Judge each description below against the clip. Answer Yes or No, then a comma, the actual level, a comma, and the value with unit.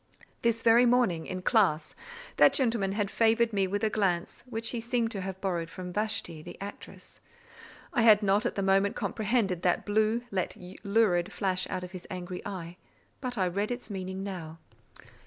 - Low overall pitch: No, high, 200 Hz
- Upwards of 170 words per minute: Yes, average, 180 wpm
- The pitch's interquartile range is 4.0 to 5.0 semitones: No, average, 3.6 semitones